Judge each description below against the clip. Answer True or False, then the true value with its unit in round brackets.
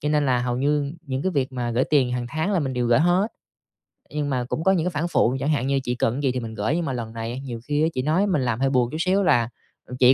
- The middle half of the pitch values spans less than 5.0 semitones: True (3.9 semitones)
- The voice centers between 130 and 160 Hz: True (135 Hz)